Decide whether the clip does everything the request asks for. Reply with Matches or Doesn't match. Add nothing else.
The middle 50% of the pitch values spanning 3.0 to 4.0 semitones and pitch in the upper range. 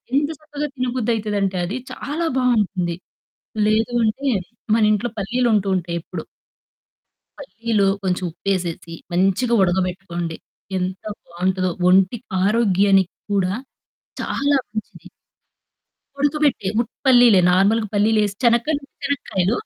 Doesn't match